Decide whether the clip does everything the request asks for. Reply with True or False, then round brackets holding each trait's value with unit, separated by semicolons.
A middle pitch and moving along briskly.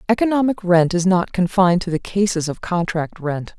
False (180 Hz; 185 wpm)